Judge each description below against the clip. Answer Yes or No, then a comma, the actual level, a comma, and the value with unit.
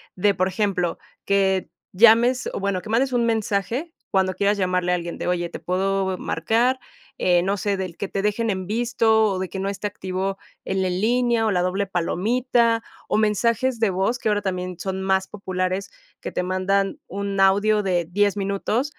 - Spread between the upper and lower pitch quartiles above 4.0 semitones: No, average, 2.9 semitones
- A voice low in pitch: No, high, 195 Hz